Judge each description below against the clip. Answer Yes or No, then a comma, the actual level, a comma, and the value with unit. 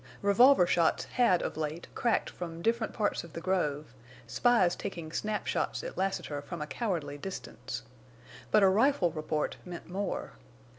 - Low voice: No, medium, 175 Hz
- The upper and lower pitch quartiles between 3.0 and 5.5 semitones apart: Yes, average, 5.1 semitones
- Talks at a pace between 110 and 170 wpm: Yes, average, 150 wpm